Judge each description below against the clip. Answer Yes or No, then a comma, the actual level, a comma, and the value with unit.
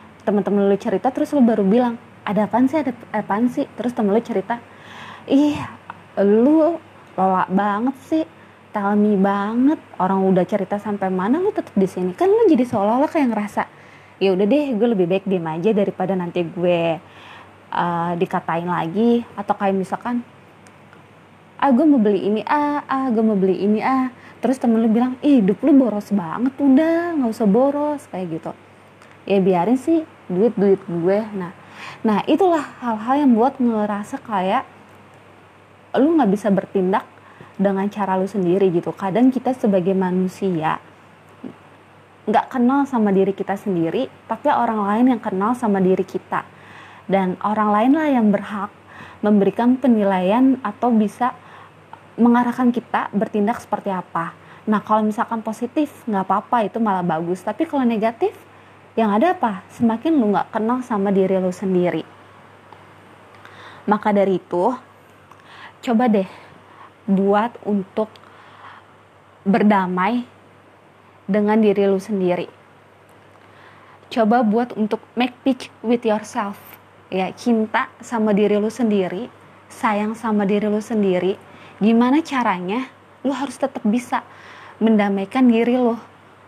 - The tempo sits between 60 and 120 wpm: No, fast, 140 wpm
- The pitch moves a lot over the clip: No, average, 4.1 semitones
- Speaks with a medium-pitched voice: No, high, 215 Hz